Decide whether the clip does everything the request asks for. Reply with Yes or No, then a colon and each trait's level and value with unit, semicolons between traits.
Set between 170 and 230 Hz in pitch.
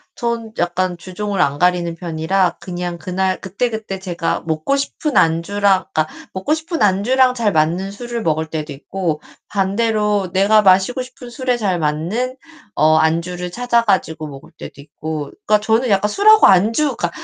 Yes: high, 190 Hz